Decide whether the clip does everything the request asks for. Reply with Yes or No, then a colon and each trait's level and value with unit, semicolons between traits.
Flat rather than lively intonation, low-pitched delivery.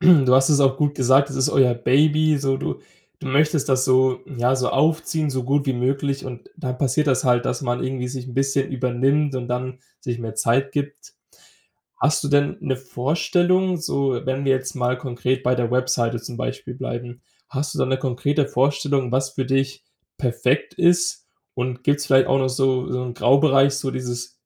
Yes: narrow, 1.9 semitones; low, 130 Hz